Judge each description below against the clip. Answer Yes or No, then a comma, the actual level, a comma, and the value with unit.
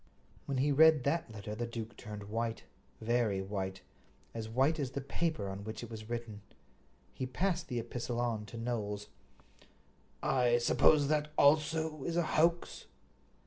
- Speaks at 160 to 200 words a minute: No, average, 150 wpm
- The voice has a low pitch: Yes, low, 120 Hz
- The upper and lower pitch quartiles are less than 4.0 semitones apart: No, average, 5.2 semitones